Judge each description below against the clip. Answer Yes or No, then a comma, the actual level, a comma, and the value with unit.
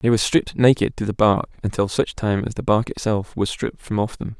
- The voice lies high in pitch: No, low, 105 Hz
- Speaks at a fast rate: Yes, fast, 260 wpm